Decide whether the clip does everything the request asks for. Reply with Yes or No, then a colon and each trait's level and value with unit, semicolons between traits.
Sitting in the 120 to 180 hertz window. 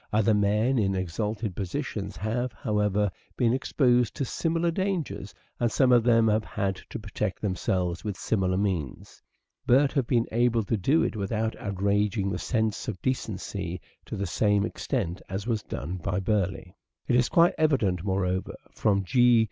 No: low, 105 Hz